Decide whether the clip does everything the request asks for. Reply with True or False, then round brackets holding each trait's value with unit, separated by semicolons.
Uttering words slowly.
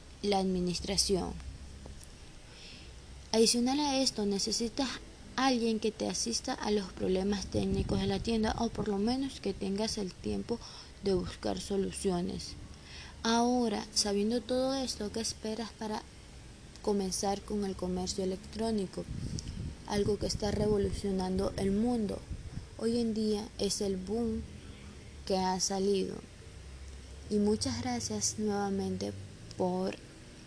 True (120 wpm)